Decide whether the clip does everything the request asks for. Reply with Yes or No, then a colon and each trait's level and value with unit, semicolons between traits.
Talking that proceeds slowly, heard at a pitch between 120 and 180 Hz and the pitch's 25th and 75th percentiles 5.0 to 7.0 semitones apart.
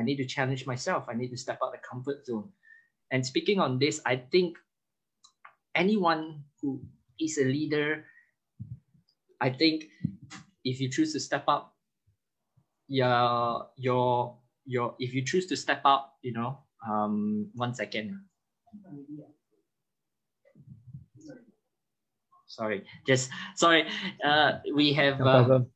No: slow, 125 wpm; medium, 140 Hz; average, 4.2 semitones